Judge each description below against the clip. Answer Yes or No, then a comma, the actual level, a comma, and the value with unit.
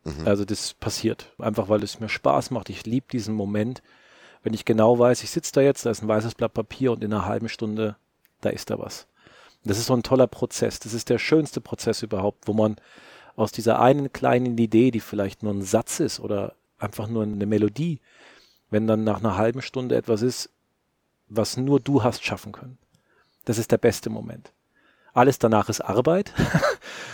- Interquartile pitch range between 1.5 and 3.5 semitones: Yes, average, 2.7 semitones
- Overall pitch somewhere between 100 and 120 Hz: Yes, low, 115 Hz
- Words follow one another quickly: Yes, fast, 195 wpm